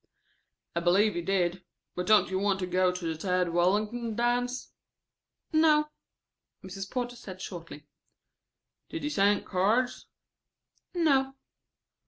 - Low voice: No, high, 200 Hz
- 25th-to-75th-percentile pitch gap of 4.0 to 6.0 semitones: Yes, average, 5.2 semitones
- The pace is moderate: No, slow, 125 wpm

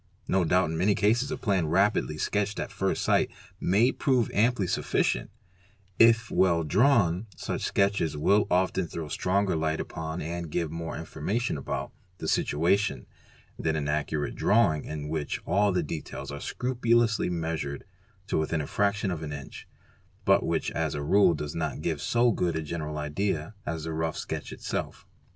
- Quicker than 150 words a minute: Yes, average, 170 wpm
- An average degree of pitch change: Yes, average, 4.7 semitones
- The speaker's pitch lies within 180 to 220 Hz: No, very low, 85 Hz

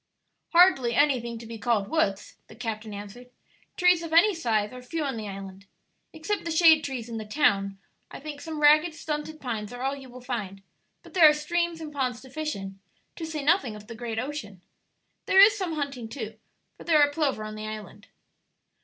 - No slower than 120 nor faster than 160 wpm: No, fast, 205 wpm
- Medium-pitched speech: No, very high, 260 Hz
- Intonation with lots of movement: Yes, wide, 6.3 semitones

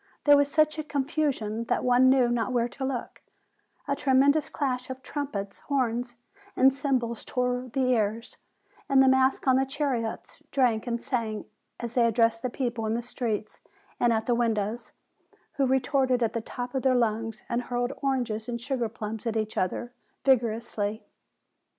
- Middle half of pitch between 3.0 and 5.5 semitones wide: No, narrow, 2.6 semitones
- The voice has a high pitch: Yes, high, 245 Hz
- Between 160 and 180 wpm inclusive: Yes, average, 175 wpm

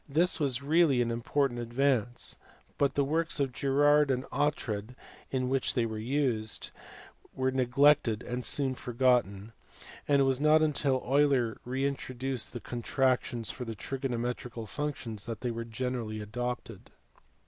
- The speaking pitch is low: Yes, low, 130 Hz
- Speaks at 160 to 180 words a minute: No, average, 140 wpm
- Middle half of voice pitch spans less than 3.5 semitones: Yes, average, 2.9 semitones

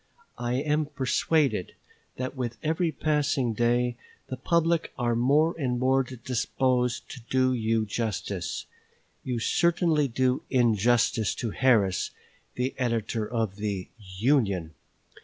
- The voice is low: Yes, low, 125 Hz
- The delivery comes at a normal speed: No, slow, 120 wpm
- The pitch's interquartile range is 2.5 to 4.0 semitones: Yes, average, 3.2 semitones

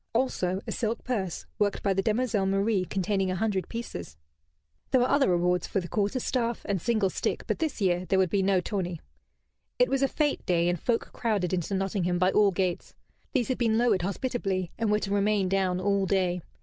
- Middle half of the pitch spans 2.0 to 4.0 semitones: Yes, average, 3.6 semitones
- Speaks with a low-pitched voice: No, high, 195 Hz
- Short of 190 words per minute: No, fast, 205 wpm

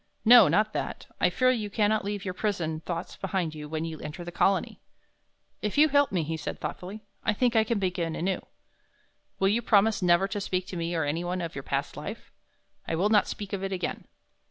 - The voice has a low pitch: No, high, 190 Hz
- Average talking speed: No, fast, 215 wpm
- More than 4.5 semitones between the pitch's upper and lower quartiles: No, average, 3.9 semitones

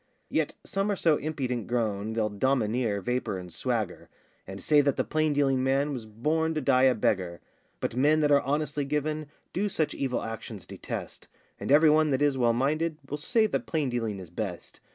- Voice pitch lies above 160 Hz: No, low, 135 Hz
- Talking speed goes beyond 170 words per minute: Yes, average, 195 wpm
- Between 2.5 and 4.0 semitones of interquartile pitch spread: No, average, 5.1 semitones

